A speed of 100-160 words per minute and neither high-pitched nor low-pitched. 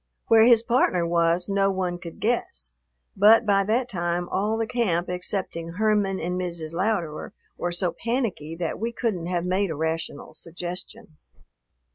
Yes: average, 155 wpm; medium, 180 Hz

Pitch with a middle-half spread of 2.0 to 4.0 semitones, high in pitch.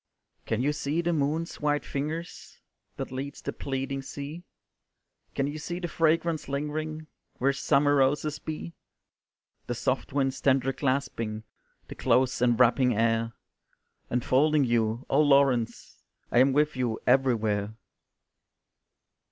No: average, 3.2 semitones; medium, 140 Hz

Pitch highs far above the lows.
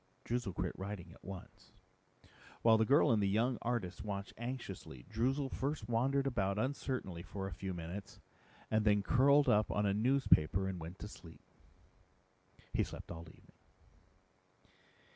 No: average, 4.3 semitones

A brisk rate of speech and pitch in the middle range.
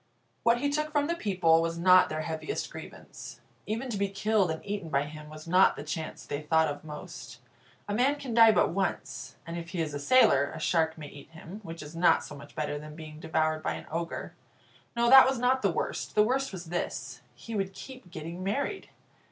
Yes: fast, 220 wpm; medium, 170 Hz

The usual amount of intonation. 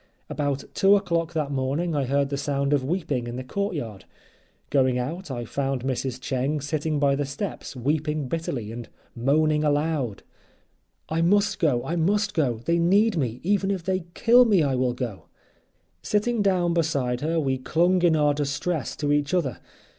Yes: average, 4.5 semitones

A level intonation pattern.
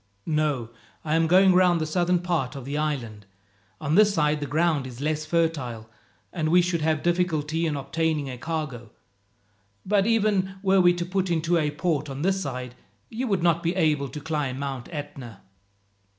No: average, 3.9 semitones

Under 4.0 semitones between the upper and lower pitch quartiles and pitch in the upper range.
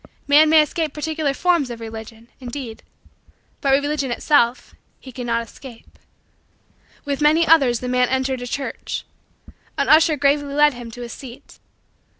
Yes: average, 3.6 semitones; very high, 275 Hz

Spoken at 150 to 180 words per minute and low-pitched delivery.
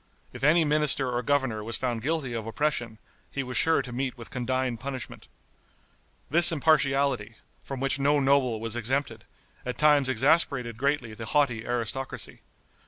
Yes: average, 155 wpm; low, 130 Hz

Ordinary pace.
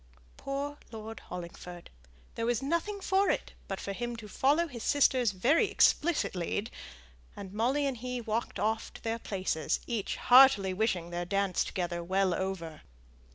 Yes: average, 155 wpm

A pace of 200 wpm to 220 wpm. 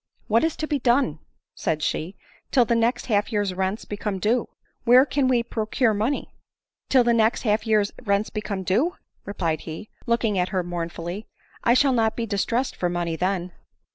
Yes: fast, 205 wpm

